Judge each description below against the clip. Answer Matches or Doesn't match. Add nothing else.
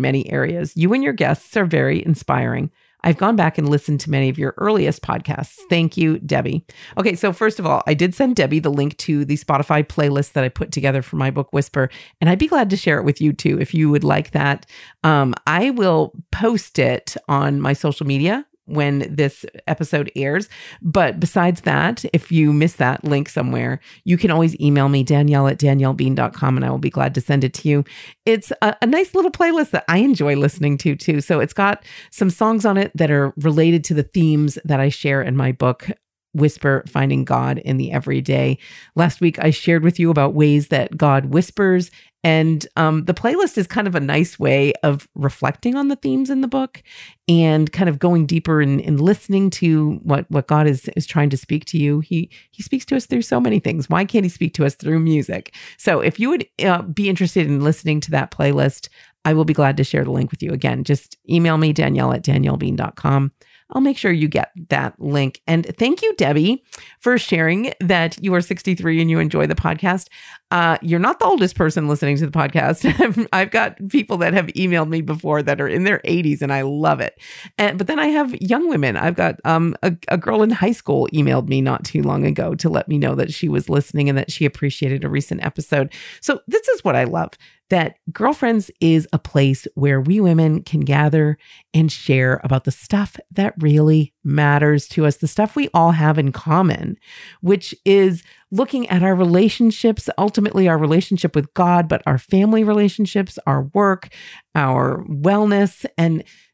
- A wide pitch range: Doesn't match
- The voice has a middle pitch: Matches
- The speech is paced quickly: Matches